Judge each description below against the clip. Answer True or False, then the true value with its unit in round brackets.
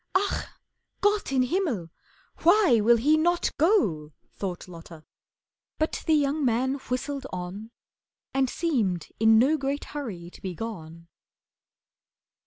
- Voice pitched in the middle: False (250 Hz)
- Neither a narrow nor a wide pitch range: False (8.8 semitones)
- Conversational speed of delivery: False (125 wpm)